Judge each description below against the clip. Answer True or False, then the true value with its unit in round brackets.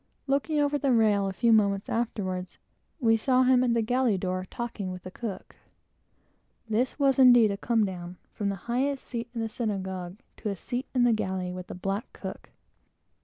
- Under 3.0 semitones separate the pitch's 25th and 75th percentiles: False (4.6 semitones)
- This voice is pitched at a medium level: False (220 Hz)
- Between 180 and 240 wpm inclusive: True (185 wpm)